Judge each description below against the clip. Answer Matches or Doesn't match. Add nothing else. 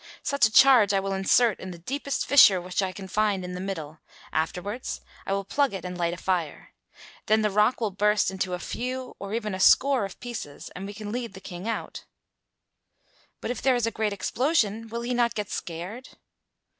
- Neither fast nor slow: Doesn't match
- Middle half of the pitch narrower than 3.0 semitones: Doesn't match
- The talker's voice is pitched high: Matches